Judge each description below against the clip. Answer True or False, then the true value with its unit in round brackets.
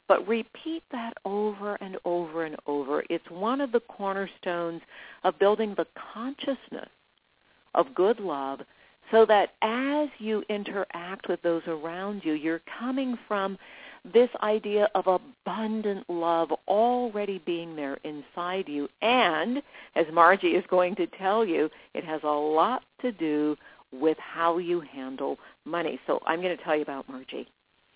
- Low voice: False (190 Hz)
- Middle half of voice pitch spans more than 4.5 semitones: True (5.2 semitones)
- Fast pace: False (150 wpm)